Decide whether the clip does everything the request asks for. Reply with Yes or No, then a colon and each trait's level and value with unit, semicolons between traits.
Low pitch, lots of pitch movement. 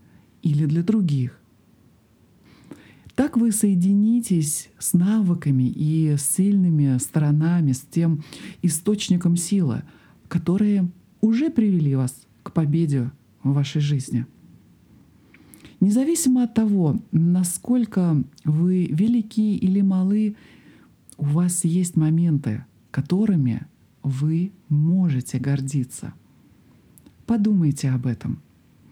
No: medium, 170 Hz; wide, 5.7 semitones